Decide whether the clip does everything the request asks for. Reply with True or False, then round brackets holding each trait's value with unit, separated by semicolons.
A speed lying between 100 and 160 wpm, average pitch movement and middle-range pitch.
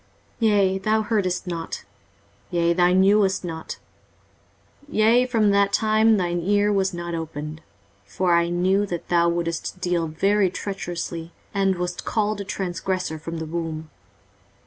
True (145 wpm; 3.0 semitones; 180 Hz)